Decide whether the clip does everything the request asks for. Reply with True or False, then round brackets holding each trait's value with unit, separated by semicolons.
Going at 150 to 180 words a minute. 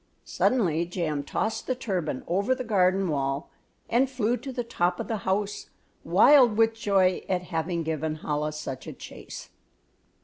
True (160 wpm)